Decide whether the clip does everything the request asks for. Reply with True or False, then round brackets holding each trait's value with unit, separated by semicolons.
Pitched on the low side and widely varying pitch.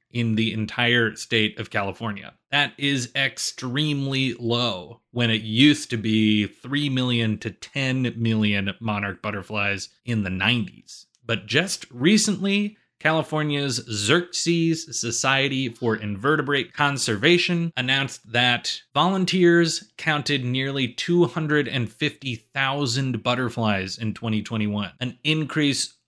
False (125 Hz; 4.7 semitones)